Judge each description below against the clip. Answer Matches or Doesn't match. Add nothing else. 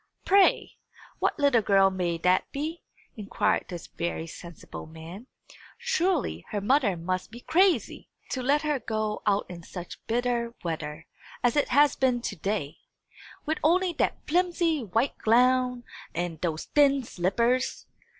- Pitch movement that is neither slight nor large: Doesn't match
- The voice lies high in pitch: Matches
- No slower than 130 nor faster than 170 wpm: Matches